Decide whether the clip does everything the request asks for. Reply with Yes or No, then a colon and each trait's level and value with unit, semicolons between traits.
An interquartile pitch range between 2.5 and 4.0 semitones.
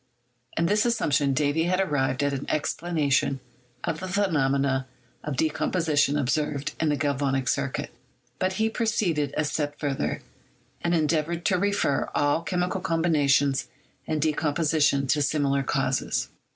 Yes: average, 3.3 semitones